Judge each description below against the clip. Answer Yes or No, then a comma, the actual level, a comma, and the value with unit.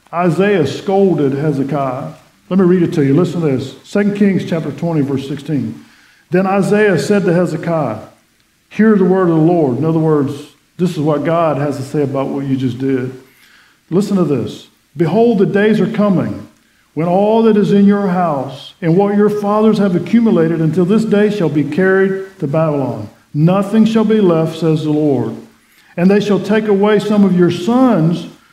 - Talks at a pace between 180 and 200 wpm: Yes, average, 185 wpm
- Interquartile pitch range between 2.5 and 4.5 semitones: No, wide, 5.6 semitones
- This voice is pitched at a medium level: Yes, medium, 170 Hz